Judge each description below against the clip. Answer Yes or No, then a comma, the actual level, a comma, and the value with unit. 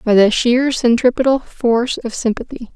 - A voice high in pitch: Yes, high, 240 Hz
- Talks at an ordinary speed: Yes, average, 150 wpm